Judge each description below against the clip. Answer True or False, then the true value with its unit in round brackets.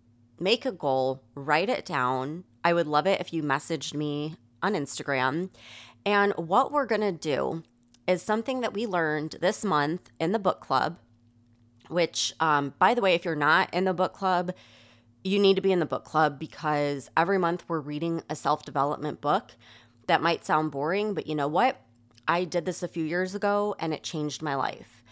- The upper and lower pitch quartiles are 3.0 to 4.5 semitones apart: False (4.9 semitones)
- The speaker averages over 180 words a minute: True (195 wpm)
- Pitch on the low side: False (160 Hz)